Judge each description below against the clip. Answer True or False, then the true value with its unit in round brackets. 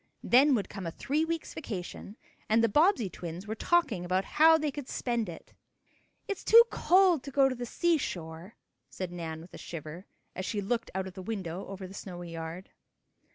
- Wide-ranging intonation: True (7.8 semitones)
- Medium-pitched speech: False (205 Hz)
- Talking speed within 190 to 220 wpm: True (195 wpm)